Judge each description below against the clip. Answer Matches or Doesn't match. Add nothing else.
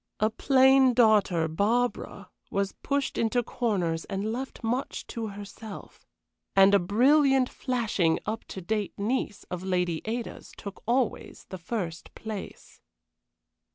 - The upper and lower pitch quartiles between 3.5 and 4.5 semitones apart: Matches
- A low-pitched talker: Doesn't match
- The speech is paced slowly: Matches